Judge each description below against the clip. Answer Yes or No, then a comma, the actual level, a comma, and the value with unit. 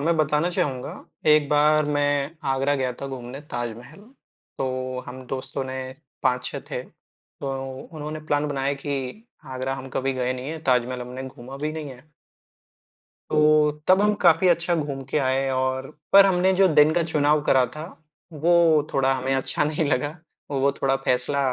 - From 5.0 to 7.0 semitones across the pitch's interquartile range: No, average, 2.7 semitones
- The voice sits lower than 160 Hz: Yes, medium, 140 Hz